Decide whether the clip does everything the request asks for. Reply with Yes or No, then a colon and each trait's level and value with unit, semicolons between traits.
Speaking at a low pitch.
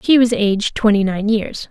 No: high, 215 Hz